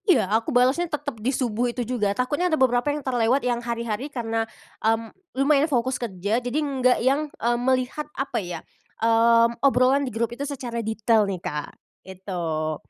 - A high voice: Yes, high, 240 Hz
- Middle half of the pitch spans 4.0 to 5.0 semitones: No, average, 3.2 semitones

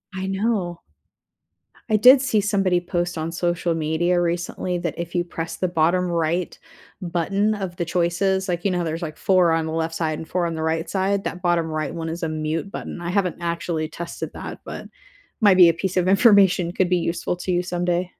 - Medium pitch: Yes, medium, 175 Hz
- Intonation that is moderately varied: No, narrow, 2.1 semitones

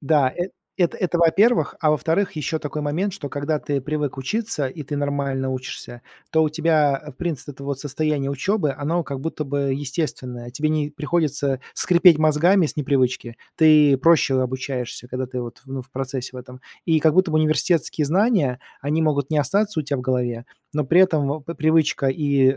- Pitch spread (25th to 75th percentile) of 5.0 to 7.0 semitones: No, average, 3.1 semitones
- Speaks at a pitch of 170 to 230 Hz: No, medium, 145 Hz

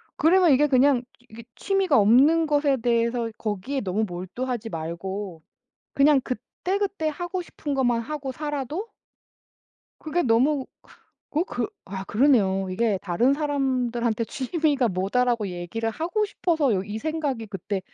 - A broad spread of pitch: Yes, wide, 5.7 semitones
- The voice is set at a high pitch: Yes, very high, 250 Hz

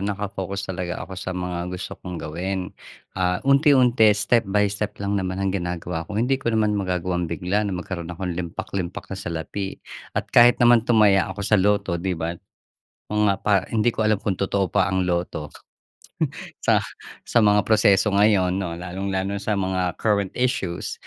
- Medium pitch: No, very low, 95 Hz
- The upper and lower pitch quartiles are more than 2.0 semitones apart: Yes, narrow, 2.5 semitones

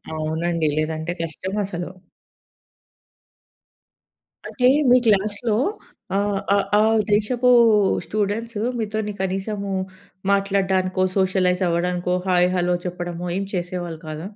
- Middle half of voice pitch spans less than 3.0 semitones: Yes, narrow, 2.6 semitones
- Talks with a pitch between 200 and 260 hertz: No, medium, 185 Hz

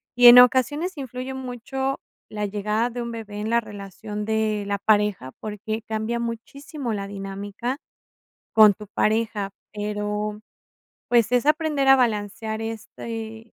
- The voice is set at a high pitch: Yes, high, 220 Hz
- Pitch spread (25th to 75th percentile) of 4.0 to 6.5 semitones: No, average, 2.9 semitones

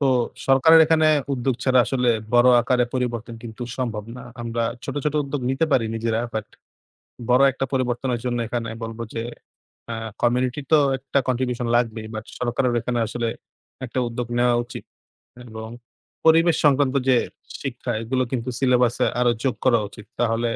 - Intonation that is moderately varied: No, narrow, 2.0 semitones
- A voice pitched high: No, low, 125 Hz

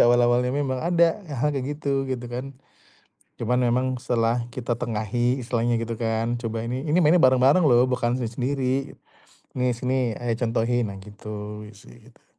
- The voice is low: Yes, low, 120 Hz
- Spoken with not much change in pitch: Yes, narrow, 2.2 semitones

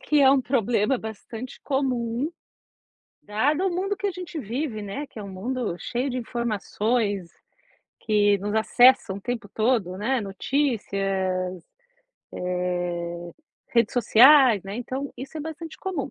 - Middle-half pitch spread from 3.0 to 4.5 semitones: No, average, 5.1 semitones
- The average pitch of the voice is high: Yes, high, 235 Hz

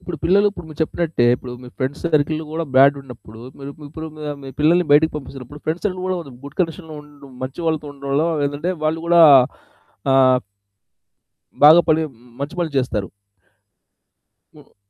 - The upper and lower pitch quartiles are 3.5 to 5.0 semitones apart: No, average, 2.9 semitones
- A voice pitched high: No, medium, 150 Hz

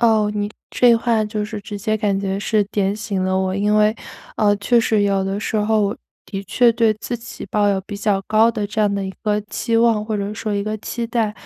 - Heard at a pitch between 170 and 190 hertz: No, high, 210 Hz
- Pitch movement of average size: No, narrow, 1.6 semitones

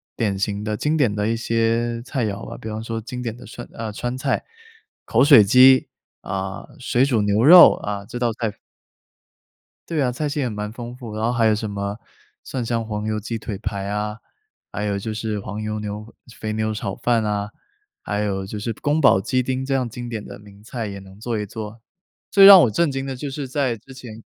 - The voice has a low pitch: Yes, low, 110 Hz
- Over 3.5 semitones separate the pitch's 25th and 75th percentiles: No, average, 3.1 semitones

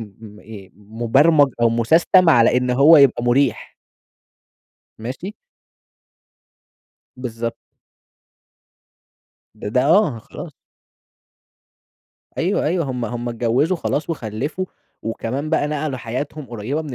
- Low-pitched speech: Yes, low, 125 Hz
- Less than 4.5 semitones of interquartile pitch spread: No, average, 4.8 semitones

